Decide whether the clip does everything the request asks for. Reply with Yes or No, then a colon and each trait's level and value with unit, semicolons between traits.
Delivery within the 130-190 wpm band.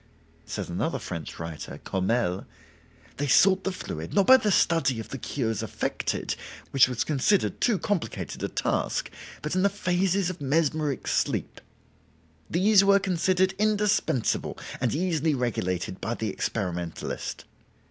Yes: slow, 135 wpm